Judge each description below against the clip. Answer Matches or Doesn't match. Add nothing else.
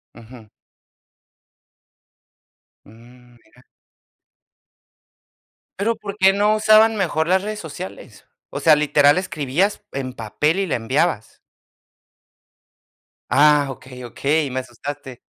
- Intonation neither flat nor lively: Doesn't match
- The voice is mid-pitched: Matches